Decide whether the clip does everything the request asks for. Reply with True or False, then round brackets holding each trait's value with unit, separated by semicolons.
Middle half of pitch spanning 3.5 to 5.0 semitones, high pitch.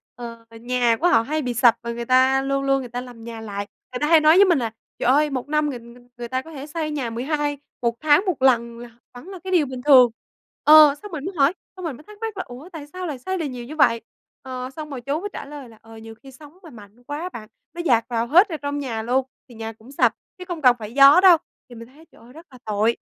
True (4.4 semitones; 270 Hz)